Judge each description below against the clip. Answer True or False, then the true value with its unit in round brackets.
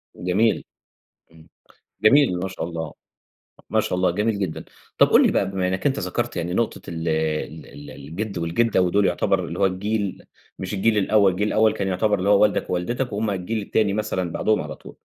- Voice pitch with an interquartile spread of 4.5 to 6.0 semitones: False (3.3 semitones)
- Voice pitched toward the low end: True (95 Hz)